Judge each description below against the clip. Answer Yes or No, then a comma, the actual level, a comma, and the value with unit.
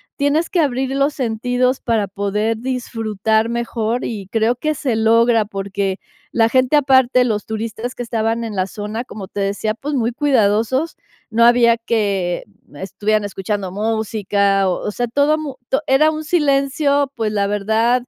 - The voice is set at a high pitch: Yes, high, 230 Hz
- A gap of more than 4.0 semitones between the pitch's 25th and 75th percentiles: No, average, 3.6 semitones